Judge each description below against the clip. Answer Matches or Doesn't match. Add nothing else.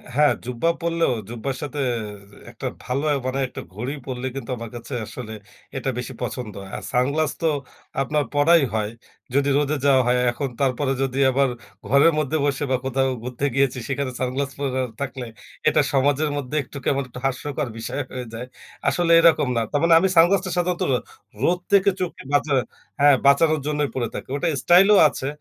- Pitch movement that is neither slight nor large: Matches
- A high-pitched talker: Doesn't match